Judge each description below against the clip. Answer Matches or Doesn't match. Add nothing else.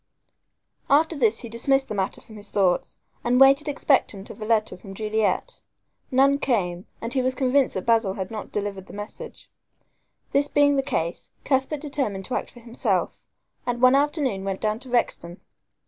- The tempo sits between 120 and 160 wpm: Doesn't match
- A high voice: Matches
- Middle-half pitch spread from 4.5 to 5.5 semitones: Matches